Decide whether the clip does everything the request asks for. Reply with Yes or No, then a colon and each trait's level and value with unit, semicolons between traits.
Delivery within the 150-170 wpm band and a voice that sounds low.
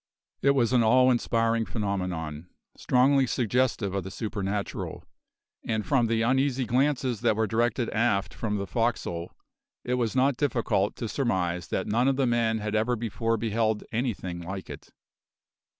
Yes: average, 155 wpm; low, 115 Hz